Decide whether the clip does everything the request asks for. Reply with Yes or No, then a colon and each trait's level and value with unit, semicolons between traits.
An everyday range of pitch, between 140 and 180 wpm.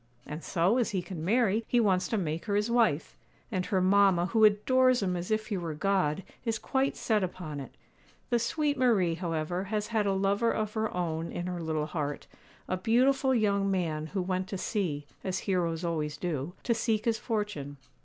No: average, 4.5 semitones; average, 200 wpm